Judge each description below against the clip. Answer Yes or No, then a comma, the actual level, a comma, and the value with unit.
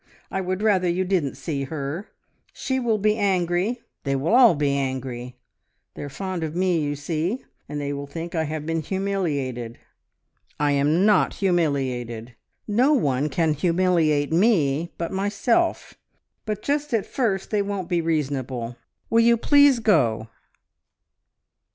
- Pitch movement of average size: No, wide, 6.1 semitones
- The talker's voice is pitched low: No, medium, 170 Hz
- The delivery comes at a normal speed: Yes, average, 150 wpm